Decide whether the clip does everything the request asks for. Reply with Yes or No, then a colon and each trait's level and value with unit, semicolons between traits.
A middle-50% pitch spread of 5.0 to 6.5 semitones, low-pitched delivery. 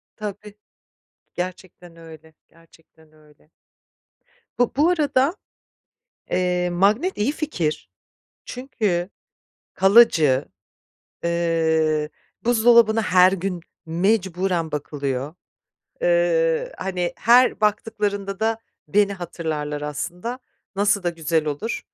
No: wide, 5.5 semitones; medium, 185 Hz